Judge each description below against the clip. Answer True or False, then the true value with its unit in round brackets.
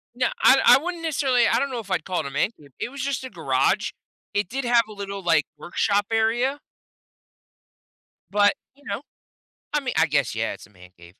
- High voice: True (215 Hz)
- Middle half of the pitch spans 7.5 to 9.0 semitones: True (7.8 semitones)